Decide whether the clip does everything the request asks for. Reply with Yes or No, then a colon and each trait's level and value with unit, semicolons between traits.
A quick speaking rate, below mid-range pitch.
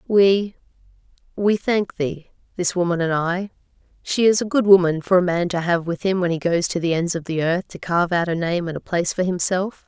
No: fast, 230 wpm; medium, 180 Hz